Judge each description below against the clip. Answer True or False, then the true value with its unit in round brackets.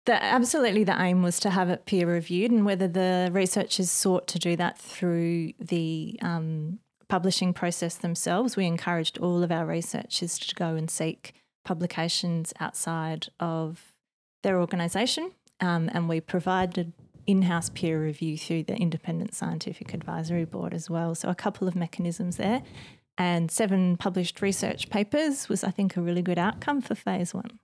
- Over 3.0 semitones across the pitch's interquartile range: False (2.6 semitones)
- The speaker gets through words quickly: False (165 wpm)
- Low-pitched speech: False (180 Hz)